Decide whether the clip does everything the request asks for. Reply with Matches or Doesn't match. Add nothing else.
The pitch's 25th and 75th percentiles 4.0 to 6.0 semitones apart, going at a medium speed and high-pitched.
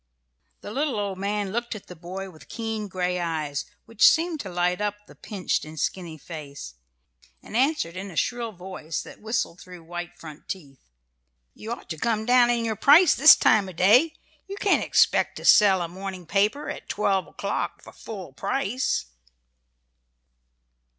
Matches